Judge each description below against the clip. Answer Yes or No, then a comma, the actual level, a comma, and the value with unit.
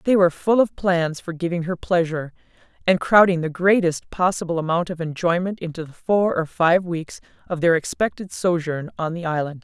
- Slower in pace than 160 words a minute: No, average, 185 wpm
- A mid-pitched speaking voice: Yes, medium, 170 Hz